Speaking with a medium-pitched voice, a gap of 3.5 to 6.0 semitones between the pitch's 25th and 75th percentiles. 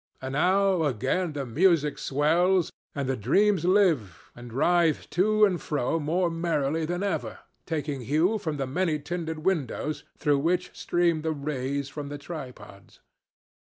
Yes: medium, 155 Hz; average, 4.1 semitones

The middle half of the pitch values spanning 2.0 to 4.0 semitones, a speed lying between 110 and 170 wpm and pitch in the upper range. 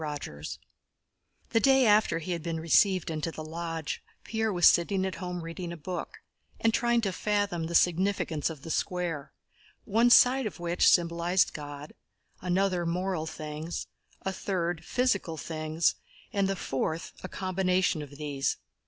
No: average, 3.2 semitones; average, 155 wpm; medium, 175 Hz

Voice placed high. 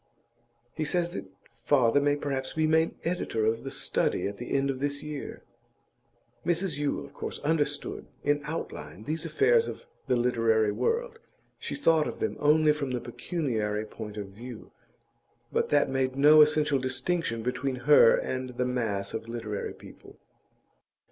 No: medium, 140 Hz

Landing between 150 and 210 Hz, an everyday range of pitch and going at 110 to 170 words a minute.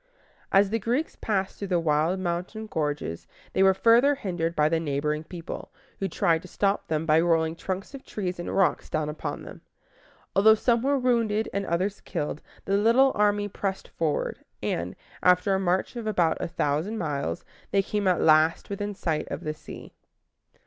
No: medium, 185 Hz; average, 4.3 semitones; average, 180 wpm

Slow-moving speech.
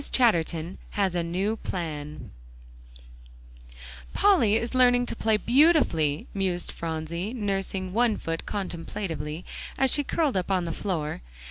Yes: slow, 125 wpm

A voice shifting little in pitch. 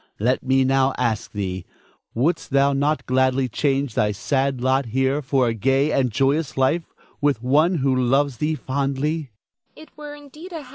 Yes: narrow, 1.9 semitones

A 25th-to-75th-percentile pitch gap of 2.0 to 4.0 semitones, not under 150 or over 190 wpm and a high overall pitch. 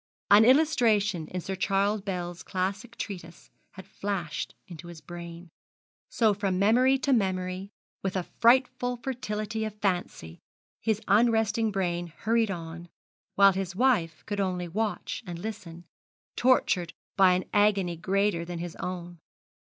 No: average, 3.7 semitones; slow, 135 wpm; high, 195 Hz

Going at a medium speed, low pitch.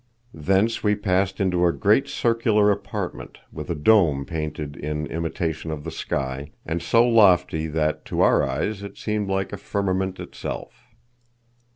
Yes: average, 155 wpm; very low, 95 Hz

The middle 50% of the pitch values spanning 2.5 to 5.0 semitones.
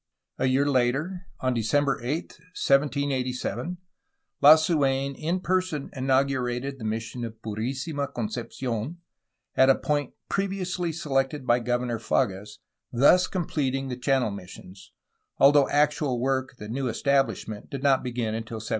Yes: average, 3.2 semitones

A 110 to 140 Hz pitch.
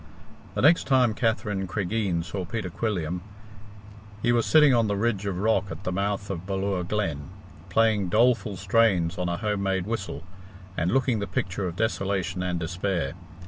No: low, 100 Hz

